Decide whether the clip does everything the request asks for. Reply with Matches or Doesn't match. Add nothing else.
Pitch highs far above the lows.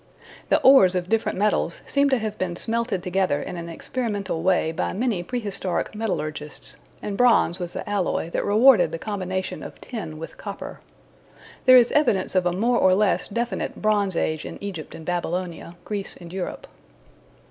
Doesn't match